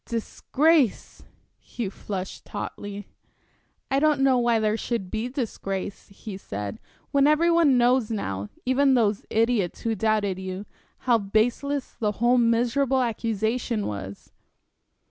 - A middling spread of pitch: Yes, average, 4.0 semitones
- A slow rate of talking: Yes, slow, 125 wpm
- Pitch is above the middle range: Yes, high, 230 Hz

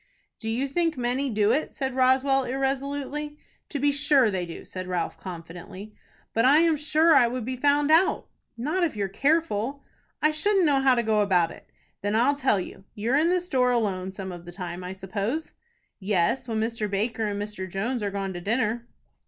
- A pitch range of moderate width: No, wide, 6.0 semitones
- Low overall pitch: No, high, 240 Hz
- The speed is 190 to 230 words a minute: Yes, average, 200 wpm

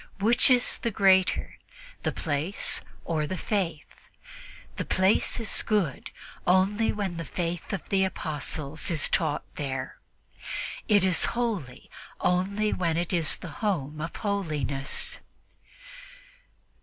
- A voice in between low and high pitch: Yes, medium, 180 Hz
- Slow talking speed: Yes, slow, 120 wpm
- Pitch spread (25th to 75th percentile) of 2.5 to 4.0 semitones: No, average, 4.6 semitones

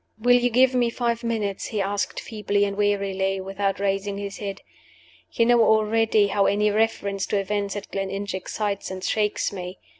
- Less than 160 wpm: No, average, 175 wpm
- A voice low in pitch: No, high, 205 Hz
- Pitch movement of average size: No, narrow, 1.9 semitones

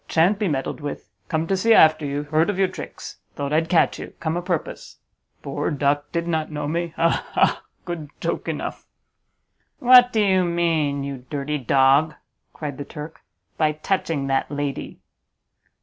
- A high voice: No, medium, 155 Hz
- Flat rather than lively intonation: No, average, 3.0 semitones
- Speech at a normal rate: Yes, average, 170 wpm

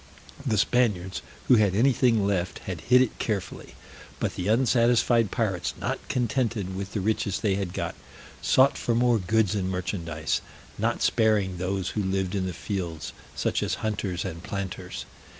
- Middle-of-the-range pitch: No, low, 100 Hz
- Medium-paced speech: Yes, average, 160 wpm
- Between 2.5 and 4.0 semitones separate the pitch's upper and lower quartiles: Yes, average, 3.6 semitones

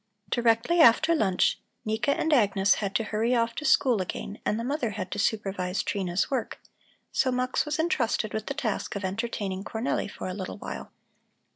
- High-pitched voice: Yes, high, 220 Hz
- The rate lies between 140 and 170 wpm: No, average, 180 wpm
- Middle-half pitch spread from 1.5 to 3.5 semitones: No, average, 4.1 semitones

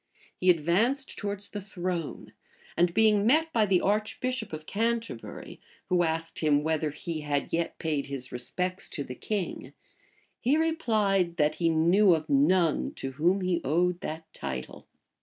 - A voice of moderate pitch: Yes, medium, 180 Hz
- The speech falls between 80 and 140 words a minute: No, average, 155 wpm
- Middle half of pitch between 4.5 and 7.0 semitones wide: Yes, average, 4.9 semitones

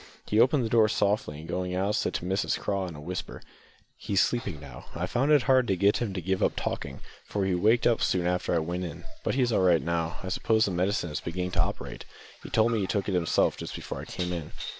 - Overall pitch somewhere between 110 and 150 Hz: No, very low, 95 Hz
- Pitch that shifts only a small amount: No, average, 3.6 semitones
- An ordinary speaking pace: No, fast, 255 wpm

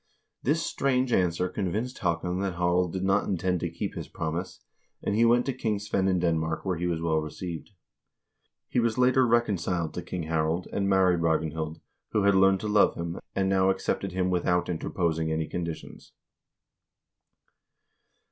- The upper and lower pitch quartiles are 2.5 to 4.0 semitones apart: Yes, average, 3.1 semitones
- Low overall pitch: Yes, very low, 90 Hz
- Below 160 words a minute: No, average, 170 wpm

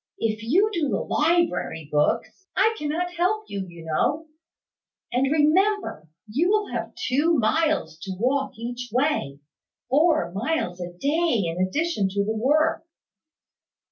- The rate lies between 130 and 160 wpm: Yes, average, 140 wpm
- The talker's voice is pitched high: Yes, very high, 270 Hz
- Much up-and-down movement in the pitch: Yes, wide, 8.6 semitones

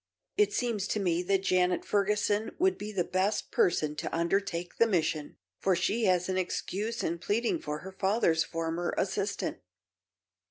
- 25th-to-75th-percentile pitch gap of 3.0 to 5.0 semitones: Yes, average, 3.3 semitones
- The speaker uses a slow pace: No, average, 160 wpm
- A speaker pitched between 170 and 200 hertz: Yes, high, 190 Hz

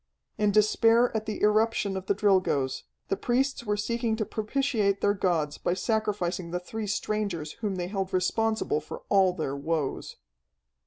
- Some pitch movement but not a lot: Yes, average, 3.5 semitones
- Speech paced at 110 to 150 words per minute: No, average, 160 wpm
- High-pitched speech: Yes, high, 205 Hz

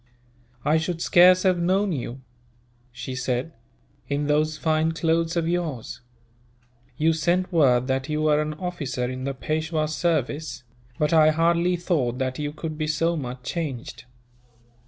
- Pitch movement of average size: Yes, average, 3.6 semitones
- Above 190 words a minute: No, average, 150 wpm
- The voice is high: No, medium, 155 Hz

